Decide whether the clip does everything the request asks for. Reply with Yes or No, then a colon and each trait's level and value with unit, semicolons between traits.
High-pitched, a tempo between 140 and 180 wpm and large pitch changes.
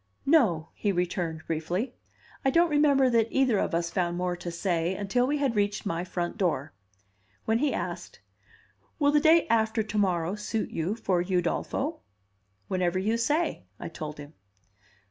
Yes: high, 195 Hz; average, 165 wpm; wide, 5.7 semitones